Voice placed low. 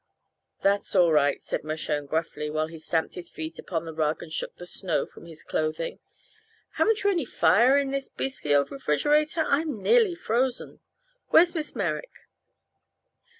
No: medium, 180 Hz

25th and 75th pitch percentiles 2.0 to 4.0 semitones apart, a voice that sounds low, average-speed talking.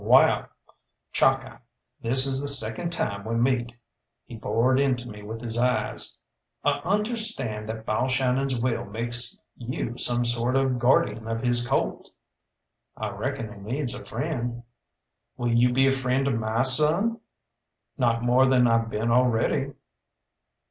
Yes: narrow, 2.4 semitones; low, 120 Hz; average, 145 wpm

